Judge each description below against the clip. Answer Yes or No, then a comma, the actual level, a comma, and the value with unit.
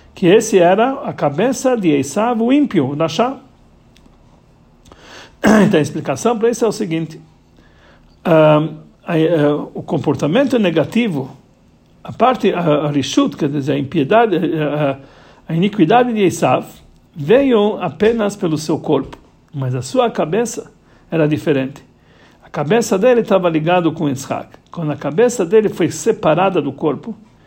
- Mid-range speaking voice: Yes, medium, 170 Hz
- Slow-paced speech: No, average, 140 wpm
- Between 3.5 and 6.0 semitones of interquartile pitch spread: No, wide, 7.1 semitones